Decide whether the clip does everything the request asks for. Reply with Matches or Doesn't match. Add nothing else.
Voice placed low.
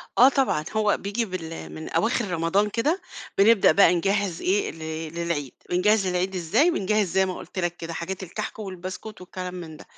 Doesn't match